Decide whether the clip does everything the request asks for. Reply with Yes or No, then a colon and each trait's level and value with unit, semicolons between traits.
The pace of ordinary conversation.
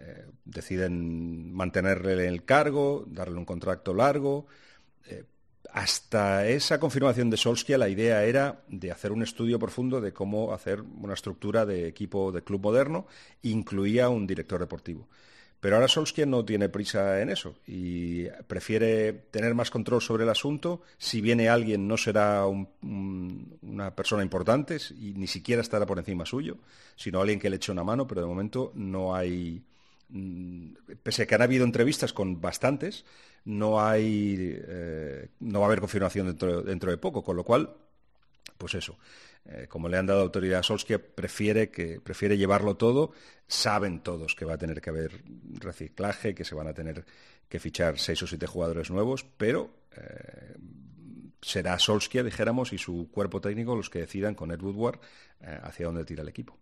Yes: average, 170 wpm